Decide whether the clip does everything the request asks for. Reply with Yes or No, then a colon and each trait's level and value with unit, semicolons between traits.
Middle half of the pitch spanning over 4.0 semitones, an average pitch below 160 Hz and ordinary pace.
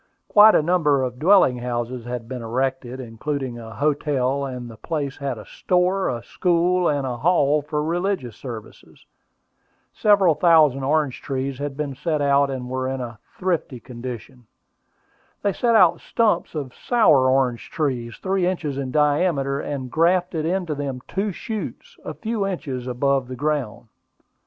Yes: average, 5.2 semitones; medium, 140 Hz; average, 155 wpm